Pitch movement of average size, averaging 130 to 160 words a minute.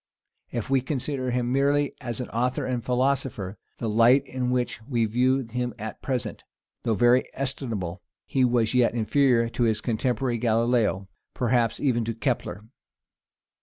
No: narrow, 2.1 semitones; average, 150 wpm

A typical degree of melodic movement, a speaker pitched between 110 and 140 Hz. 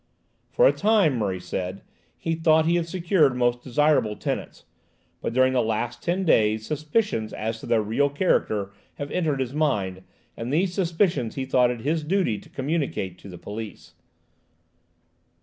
No: wide, 6.8 semitones; low, 135 Hz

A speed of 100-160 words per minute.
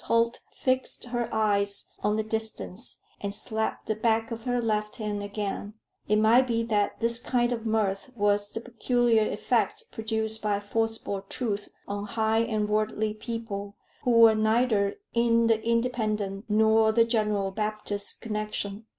Yes: average, 150 wpm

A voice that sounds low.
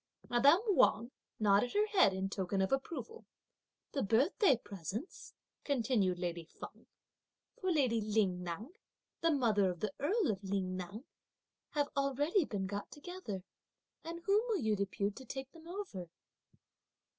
No: high, 230 Hz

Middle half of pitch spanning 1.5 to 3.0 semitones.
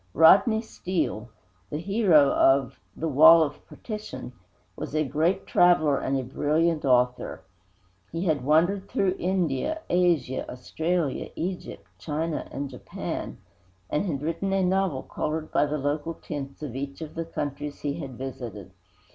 No: average, 4.3 semitones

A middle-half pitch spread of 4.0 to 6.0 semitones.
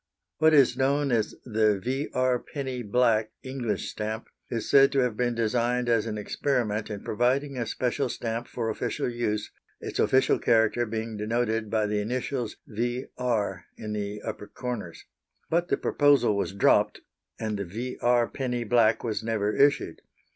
No: average, 2.8 semitones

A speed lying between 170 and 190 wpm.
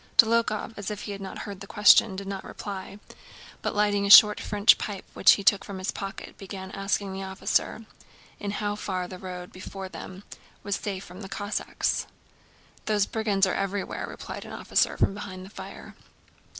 Yes: average, 180 wpm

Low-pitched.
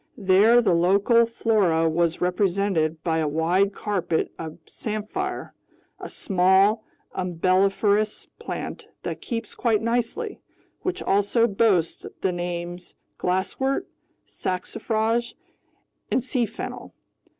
No: high, 195 Hz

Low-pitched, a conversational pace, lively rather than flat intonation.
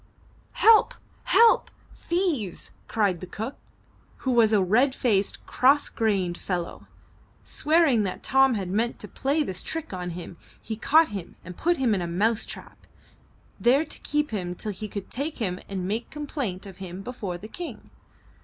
No: high, 215 Hz; average, 170 wpm; wide, 6.7 semitones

